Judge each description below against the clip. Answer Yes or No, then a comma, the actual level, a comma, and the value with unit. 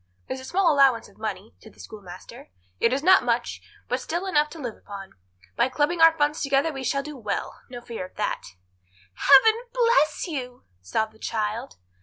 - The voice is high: Yes, very high, 265 Hz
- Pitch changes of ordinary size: No, wide, 5.9 semitones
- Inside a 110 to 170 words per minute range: No, average, 190 wpm